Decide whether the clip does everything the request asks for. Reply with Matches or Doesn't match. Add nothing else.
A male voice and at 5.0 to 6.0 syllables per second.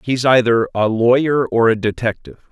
Matches